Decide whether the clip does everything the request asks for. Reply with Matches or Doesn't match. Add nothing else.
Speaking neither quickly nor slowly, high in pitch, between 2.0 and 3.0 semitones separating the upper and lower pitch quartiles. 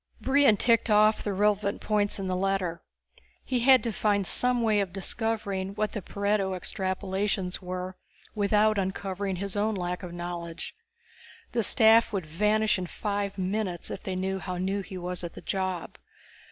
Matches